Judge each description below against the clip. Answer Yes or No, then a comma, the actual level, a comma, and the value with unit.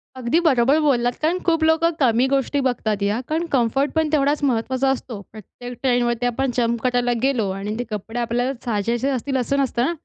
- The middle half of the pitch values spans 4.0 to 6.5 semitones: No, average, 2.8 semitones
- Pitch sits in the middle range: No, very high, 250 Hz